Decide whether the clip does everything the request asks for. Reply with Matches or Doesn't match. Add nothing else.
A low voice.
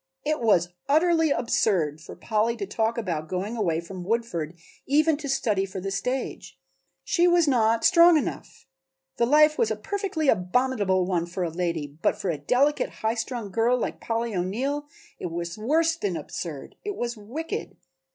Doesn't match